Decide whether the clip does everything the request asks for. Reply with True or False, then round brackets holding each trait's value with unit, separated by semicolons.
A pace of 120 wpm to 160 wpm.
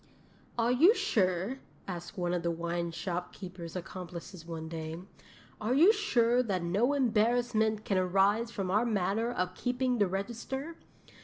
True (145 wpm)